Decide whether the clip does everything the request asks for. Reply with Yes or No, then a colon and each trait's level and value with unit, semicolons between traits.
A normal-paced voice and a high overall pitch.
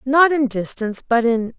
Yes: average, 190 wpm; very high, 255 Hz